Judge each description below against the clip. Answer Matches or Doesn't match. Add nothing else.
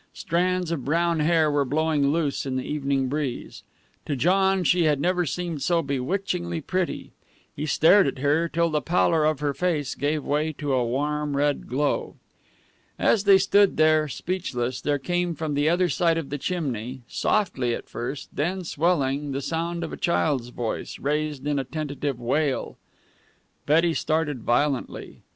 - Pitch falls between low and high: Matches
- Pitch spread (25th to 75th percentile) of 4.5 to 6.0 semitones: Doesn't match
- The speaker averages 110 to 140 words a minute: Doesn't match